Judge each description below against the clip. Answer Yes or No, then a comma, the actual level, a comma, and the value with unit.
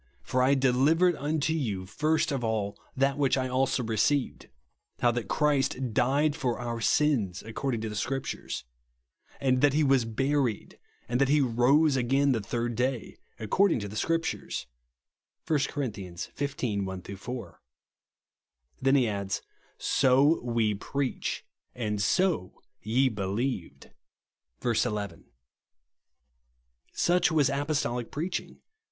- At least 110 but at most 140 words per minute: Yes, slow, 135 wpm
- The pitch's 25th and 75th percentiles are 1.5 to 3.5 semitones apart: No, average, 4.3 semitones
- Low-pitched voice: Yes, low, 130 Hz